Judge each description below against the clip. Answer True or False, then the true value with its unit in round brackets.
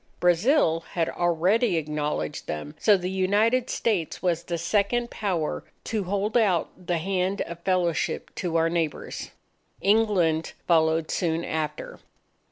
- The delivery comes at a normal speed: False (130 wpm)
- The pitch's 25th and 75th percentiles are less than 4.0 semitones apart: True (3.6 semitones)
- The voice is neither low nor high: True (175 Hz)